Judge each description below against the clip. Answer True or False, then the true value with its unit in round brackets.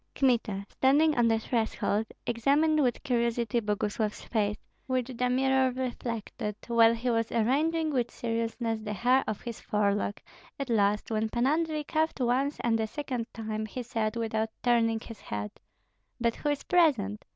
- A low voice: False (235 Hz)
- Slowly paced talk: False (160 wpm)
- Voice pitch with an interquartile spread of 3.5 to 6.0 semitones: False (3.1 semitones)